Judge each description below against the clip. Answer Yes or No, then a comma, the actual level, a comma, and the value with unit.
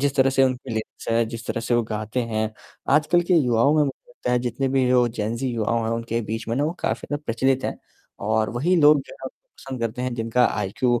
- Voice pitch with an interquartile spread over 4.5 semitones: No, average, 2.7 semitones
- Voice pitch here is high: No, low, 125 Hz